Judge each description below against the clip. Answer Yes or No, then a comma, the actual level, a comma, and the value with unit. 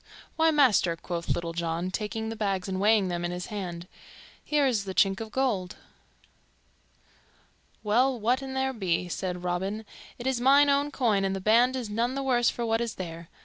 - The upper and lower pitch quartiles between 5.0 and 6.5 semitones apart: Yes, wide, 5.5 semitones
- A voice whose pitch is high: Yes, high, 215 Hz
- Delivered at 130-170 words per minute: No, average, 190 wpm